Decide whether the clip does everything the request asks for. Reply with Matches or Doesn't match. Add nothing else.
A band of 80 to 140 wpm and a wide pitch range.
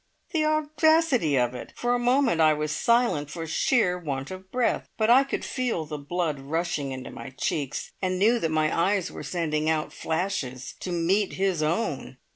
Doesn't match